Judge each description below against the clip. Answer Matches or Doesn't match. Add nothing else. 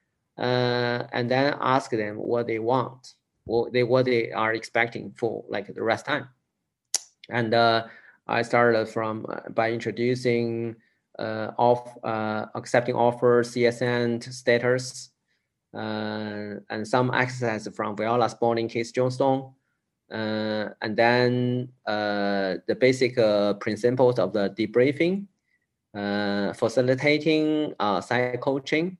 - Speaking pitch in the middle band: Doesn't match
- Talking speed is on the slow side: Matches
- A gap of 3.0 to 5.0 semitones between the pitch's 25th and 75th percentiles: Doesn't match